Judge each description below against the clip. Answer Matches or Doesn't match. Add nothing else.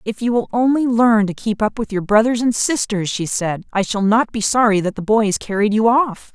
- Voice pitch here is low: Doesn't match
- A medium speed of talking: Doesn't match